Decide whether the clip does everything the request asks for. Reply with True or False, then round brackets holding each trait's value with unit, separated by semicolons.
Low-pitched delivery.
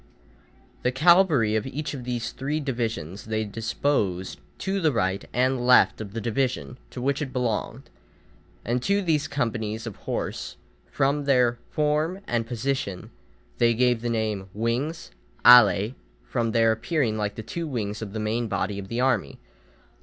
True (120 Hz)